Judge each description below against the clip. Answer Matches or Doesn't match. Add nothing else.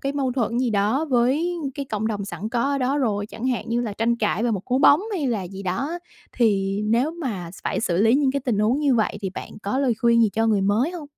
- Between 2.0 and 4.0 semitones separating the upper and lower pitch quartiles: Doesn't match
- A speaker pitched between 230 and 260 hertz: Matches